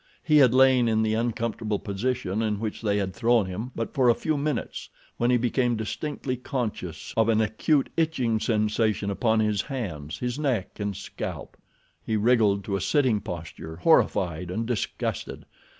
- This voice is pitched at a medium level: No, low, 110 Hz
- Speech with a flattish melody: No, average, 3.5 semitones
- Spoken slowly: No, average, 165 wpm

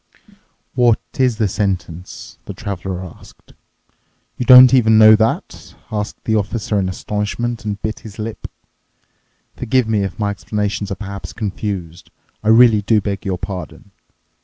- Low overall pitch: Yes, low, 105 Hz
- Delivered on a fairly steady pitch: Yes, narrow, 2.3 semitones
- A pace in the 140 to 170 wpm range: Yes, average, 145 wpm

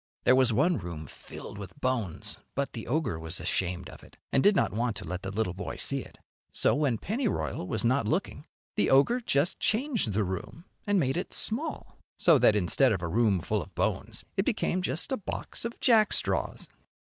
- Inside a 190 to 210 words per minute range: Yes, average, 200 wpm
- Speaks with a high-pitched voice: No, low, 130 Hz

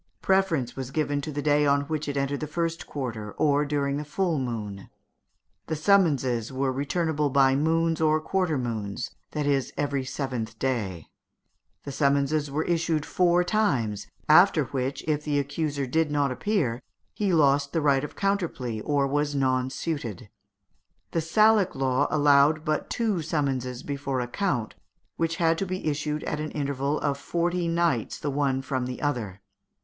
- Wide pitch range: No, average, 3.4 semitones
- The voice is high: No, medium, 145 Hz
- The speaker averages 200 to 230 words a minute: No, average, 165 wpm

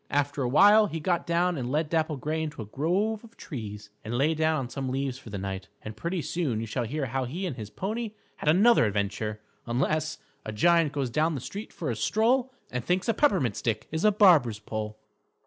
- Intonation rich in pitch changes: Yes, wide, 7.0 semitones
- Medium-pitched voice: Yes, medium, 150 Hz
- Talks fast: Yes, fast, 220 wpm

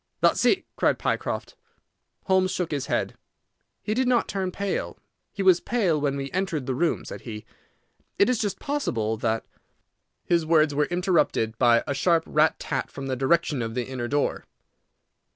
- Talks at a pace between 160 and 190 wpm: Yes, average, 170 wpm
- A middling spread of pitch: No, wide, 6.2 semitones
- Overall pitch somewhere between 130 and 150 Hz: No, medium, 160 Hz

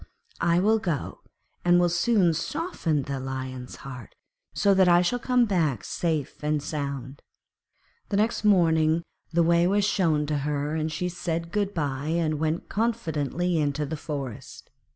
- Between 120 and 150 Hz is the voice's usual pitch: No, medium, 160 Hz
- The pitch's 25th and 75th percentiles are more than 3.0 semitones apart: Yes, average, 3.6 semitones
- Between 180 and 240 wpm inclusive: No, average, 155 wpm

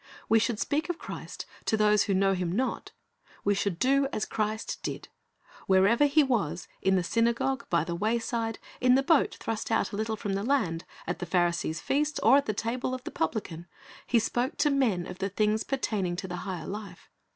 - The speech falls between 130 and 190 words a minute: No, average, 200 wpm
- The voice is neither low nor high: No, high, 215 Hz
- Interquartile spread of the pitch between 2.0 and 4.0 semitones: No, average, 5.0 semitones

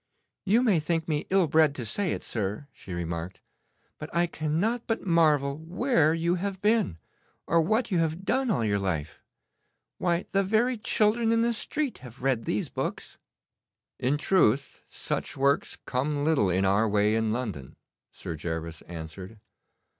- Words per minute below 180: Yes, average, 160 wpm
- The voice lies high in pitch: No, medium, 150 Hz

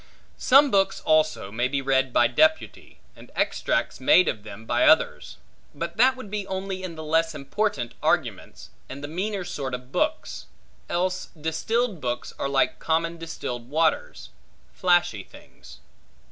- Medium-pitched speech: Yes, medium, 160 Hz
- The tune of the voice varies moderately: No, wide, 6.5 semitones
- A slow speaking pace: No, average, 150 wpm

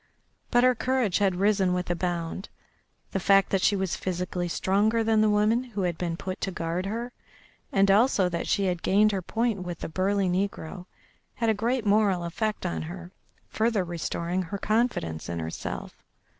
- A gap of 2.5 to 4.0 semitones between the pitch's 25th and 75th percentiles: Yes, average, 3.3 semitones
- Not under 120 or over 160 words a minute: No, average, 185 wpm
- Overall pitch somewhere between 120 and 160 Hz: No, high, 195 Hz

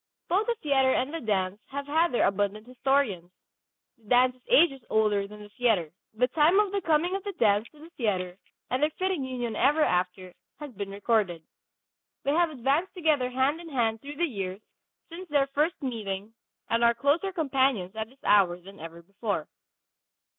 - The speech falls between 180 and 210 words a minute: Yes, average, 185 wpm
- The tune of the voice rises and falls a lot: Yes, wide, 6.6 semitones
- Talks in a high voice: Yes, very high, 250 Hz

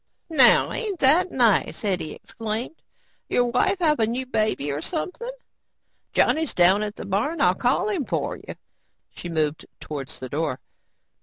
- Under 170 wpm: Yes, average, 155 wpm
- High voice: Yes, high, 230 Hz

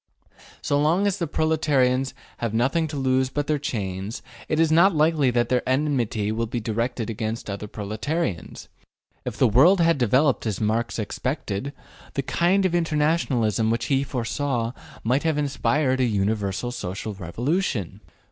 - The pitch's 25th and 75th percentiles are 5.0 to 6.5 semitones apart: Yes, average, 5.3 semitones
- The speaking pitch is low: Yes, low, 130 Hz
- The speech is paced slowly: No, average, 155 wpm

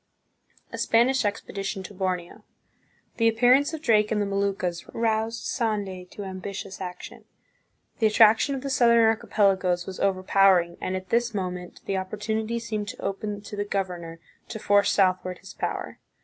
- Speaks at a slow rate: No, average, 160 wpm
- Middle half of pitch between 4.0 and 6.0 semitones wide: No, average, 3.1 semitones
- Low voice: No, high, 205 Hz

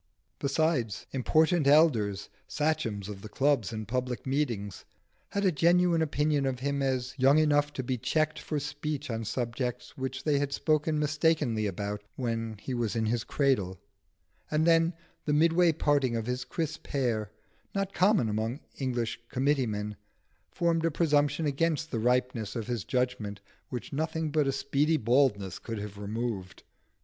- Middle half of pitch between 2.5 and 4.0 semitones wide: No, average, 5.1 semitones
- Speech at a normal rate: Yes, average, 160 wpm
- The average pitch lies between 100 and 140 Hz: Yes, low, 135 Hz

